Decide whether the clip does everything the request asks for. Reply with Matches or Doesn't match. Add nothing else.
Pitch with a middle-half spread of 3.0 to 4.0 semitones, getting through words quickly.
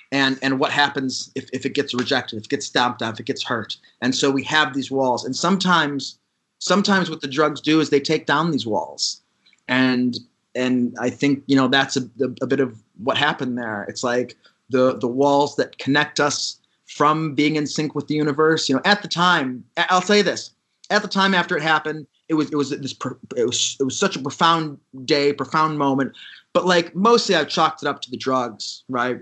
Matches